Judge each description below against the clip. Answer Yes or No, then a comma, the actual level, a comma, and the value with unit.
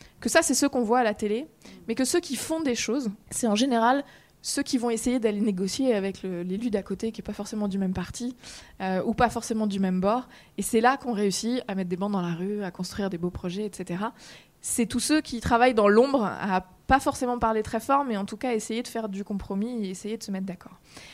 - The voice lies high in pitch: Yes, high, 220 Hz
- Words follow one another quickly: Yes, fast, 255 wpm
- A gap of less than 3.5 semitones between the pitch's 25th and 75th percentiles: No, average, 3.9 semitones